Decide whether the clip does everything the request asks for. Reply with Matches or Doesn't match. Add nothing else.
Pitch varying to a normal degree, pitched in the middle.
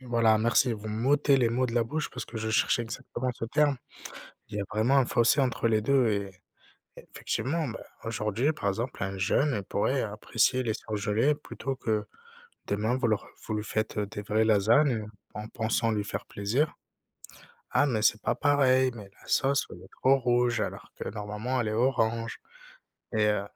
Doesn't match